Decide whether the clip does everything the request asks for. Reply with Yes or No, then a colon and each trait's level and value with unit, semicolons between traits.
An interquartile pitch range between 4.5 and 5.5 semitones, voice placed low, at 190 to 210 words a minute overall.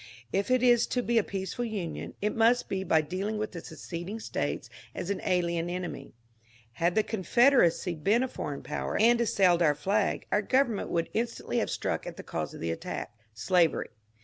No: average, 5.1 semitones; high, 195 Hz; average, 195 wpm